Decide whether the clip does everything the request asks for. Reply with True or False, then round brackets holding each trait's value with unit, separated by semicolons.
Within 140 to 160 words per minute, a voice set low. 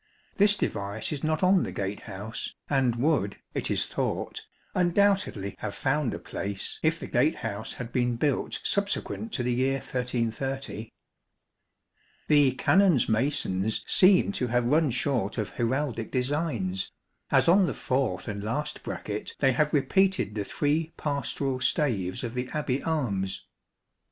True (145 wpm; 130 Hz)